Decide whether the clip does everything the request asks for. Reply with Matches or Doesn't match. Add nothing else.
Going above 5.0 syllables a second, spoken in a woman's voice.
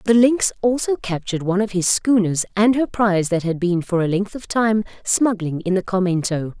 Matches